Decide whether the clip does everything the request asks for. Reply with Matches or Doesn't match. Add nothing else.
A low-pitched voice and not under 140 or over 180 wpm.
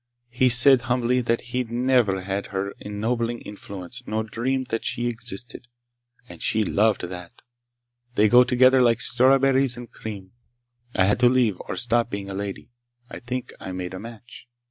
Matches